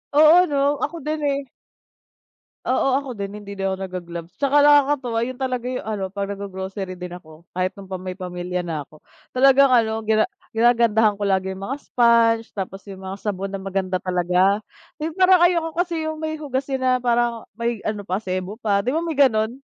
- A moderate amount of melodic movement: No, wide, 5.8 semitones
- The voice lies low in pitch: No, high, 220 Hz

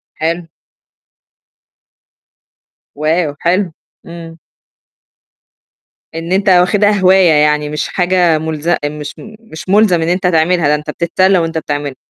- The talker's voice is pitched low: No, medium, 170 Hz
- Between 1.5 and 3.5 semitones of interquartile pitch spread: Yes, average, 2.9 semitones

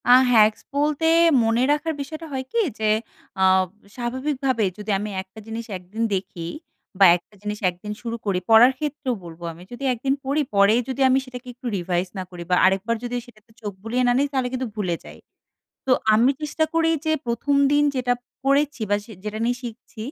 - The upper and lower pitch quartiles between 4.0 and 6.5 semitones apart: Yes, average, 4.3 semitones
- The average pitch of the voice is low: No, high, 240 Hz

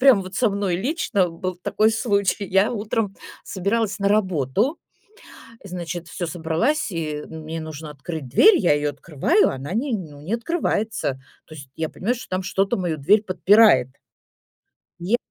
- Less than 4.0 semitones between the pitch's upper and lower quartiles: No, average, 5.2 semitones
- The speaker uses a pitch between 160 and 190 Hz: Yes, medium, 185 Hz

